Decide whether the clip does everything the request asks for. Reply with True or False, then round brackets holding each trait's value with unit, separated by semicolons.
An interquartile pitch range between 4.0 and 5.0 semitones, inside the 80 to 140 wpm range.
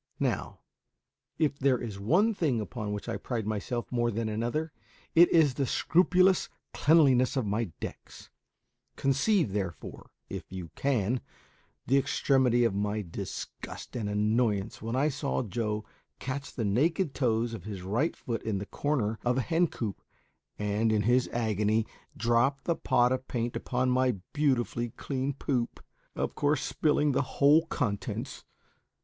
False (4.5 semitones; 150 wpm)